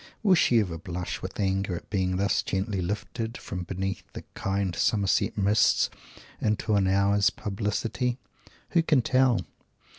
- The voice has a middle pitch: No, low, 100 Hz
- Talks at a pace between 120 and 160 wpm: Yes, average, 150 wpm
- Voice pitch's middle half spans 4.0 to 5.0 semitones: No, average, 2.8 semitones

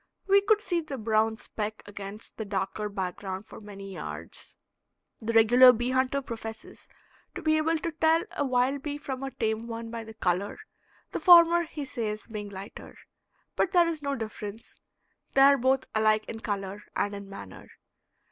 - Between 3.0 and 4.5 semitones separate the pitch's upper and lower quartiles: No, average, 5.1 semitones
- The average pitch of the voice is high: Yes, high, 230 Hz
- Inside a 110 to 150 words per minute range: No, average, 175 wpm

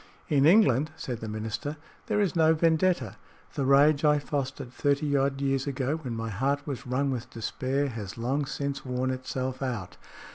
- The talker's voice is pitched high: No, low, 135 Hz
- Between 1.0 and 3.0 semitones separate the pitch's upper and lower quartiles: Yes, narrow, 2.5 semitones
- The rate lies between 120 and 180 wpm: Yes, average, 175 wpm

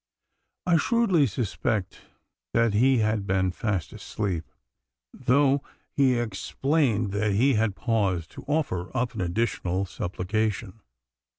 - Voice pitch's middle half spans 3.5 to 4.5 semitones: No, average, 5.0 semitones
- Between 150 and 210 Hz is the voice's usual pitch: No, low, 110 Hz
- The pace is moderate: No, slow, 115 wpm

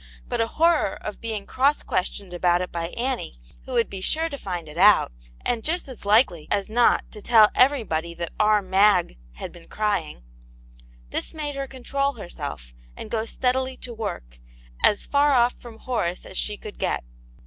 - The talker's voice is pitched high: Yes, high, 210 Hz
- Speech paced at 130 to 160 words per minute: No, average, 185 wpm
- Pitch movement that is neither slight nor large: No, wide, 6.4 semitones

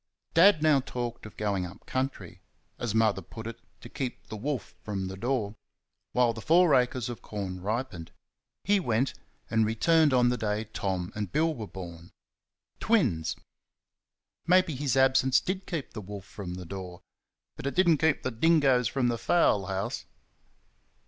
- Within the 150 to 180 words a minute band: Yes, average, 170 wpm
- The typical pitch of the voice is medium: No, low, 120 Hz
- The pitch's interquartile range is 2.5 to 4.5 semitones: No, wide, 5.5 semitones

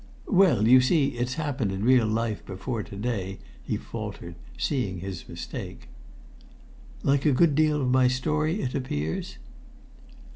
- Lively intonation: Yes, wide, 5.8 semitones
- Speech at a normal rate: Yes, average, 145 wpm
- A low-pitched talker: Yes, low, 125 Hz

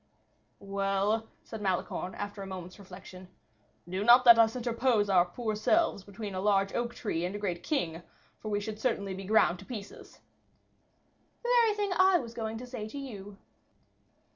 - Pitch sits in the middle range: No, high, 210 Hz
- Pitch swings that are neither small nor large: Yes, average, 3.6 semitones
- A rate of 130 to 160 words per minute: No, average, 175 wpm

